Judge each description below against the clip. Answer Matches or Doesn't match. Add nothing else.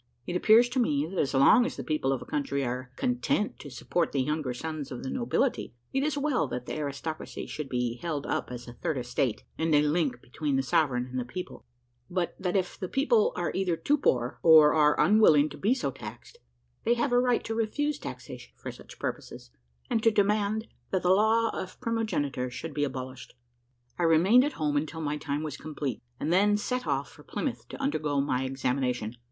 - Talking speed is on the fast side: Matches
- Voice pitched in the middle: Matches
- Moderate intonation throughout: Doesn't match